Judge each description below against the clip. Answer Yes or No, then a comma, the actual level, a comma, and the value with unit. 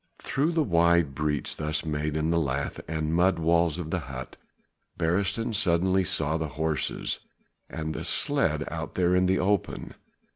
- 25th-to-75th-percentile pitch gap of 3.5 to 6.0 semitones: No, average, 3.0 semitones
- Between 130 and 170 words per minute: Yes, average, 160 wpm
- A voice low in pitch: Yes, very low, 85 Hz